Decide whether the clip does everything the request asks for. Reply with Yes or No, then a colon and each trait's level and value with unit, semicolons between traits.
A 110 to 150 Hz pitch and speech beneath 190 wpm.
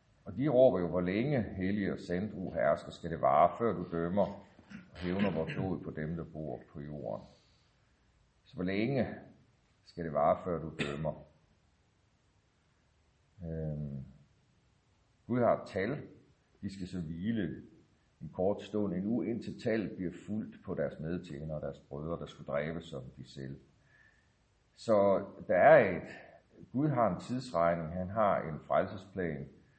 No: very low, 85 Hz; average, 150 wpm